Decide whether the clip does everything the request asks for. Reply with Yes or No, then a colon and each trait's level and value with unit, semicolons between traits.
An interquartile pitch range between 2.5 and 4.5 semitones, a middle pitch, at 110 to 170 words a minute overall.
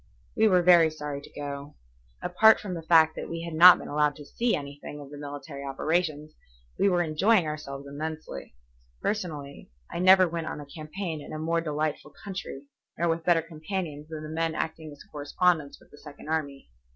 No: average, 2.8 semitones; medium, 155 Hz; average, 190 wpm